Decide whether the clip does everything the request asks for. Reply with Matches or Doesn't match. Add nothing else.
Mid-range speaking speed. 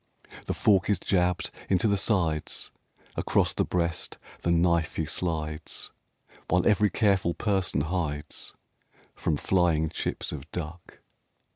Doesn't match